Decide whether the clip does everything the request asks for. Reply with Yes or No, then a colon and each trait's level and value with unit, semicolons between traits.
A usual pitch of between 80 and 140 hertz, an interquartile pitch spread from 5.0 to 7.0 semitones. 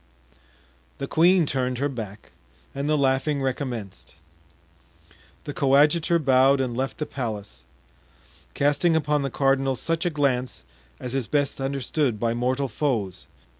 No: low, 135 Hz; narrow, 2.6 semitones